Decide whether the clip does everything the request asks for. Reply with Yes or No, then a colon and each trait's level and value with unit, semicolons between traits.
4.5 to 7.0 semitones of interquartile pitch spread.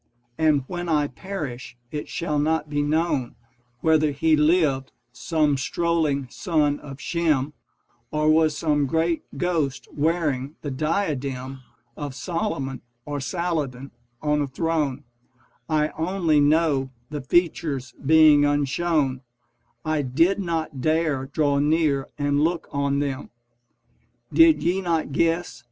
No: average, 2.7 semitones